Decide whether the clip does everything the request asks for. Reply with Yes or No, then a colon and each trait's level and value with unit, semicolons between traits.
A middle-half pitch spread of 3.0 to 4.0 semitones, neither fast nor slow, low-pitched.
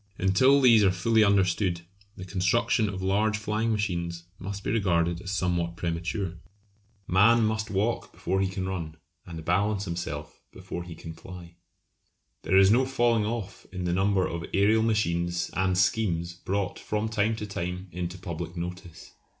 Yes: average, 3.5 semitones; average, 160 wpm; very low, 95 Hz